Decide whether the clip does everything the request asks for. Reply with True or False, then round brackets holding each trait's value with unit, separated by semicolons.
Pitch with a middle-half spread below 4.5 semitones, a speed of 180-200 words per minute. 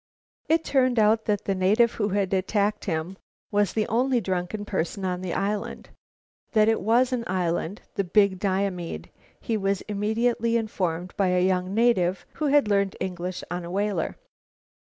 False (3.1 semitones; 165 wpm)